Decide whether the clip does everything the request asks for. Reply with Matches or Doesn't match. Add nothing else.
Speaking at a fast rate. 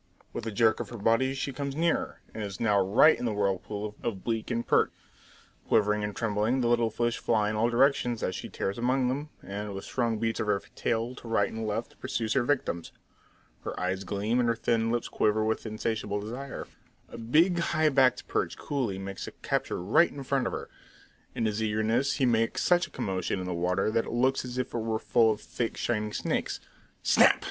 Matches